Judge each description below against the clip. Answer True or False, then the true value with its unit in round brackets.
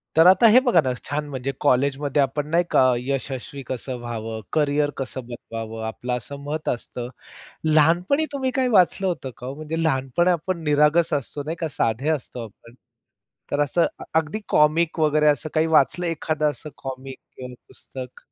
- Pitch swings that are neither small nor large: True (3.8 semitones)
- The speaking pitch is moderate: True (145 Hz)